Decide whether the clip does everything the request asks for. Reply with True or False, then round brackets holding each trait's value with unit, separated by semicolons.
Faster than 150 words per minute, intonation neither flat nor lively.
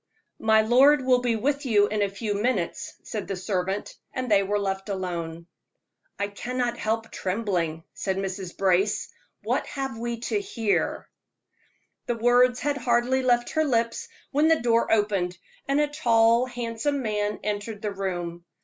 True (160 wpm; 4.0 semitones)